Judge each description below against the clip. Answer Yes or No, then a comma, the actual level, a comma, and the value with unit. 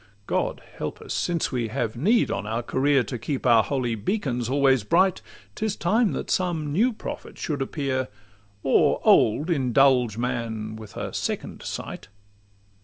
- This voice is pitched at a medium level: No, low, 130 Hz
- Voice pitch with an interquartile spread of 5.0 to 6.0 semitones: Yes, wide, 5.5 semitones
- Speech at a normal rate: Yes, average, 155 wpm